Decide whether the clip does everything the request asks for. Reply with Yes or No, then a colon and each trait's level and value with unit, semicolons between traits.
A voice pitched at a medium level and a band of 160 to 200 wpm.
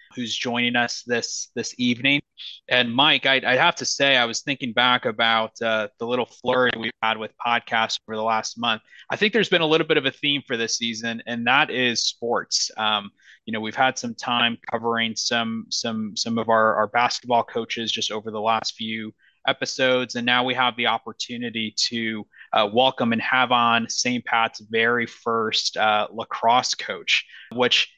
No: low, 120 Hz; average, 190 wpm